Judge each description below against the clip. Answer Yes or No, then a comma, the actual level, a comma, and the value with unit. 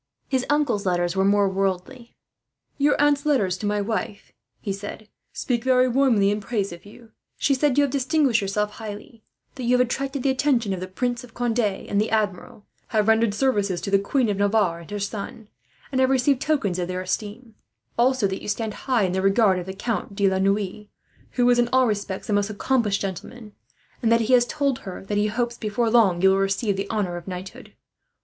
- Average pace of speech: No, fast, 215 wpm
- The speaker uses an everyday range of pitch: Yes, average, 3.9 semitones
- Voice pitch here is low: No, high, 215 Hz